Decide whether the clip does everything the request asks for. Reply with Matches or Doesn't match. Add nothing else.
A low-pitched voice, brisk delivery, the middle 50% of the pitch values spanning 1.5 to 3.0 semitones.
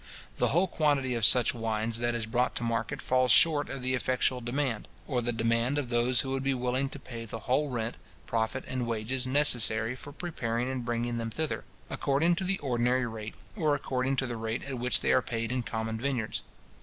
Matches